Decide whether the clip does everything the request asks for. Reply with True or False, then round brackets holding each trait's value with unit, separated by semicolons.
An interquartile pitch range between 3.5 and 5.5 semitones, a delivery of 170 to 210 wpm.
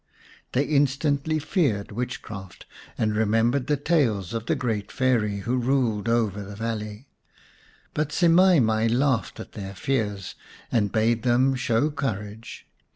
False (4.5 semitones; 140 wpm)